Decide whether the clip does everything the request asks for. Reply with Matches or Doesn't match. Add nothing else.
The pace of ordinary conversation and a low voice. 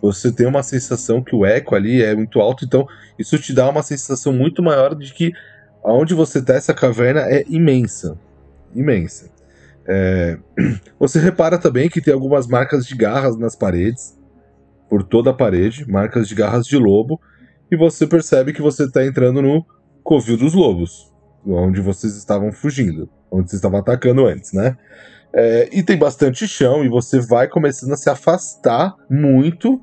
Matches